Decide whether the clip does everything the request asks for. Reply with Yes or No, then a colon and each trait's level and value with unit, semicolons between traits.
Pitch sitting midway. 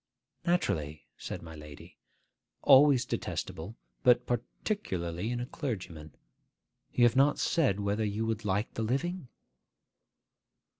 No: low, 110 Hz